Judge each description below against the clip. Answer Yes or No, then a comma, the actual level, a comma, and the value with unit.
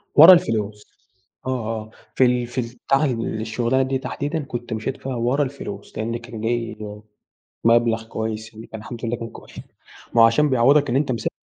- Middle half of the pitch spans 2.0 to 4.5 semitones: Yes, average, 2.8 semitones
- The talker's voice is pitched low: Yes, low, 120 Hz